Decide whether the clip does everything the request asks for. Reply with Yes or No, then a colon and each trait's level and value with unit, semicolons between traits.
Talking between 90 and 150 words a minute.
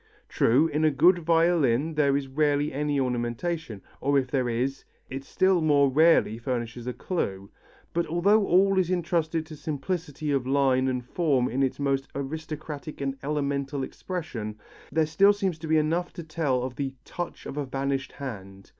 No: average, 170 wpm